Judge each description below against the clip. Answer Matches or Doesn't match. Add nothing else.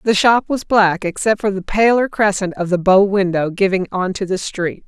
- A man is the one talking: Doesn't match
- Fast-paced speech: Matches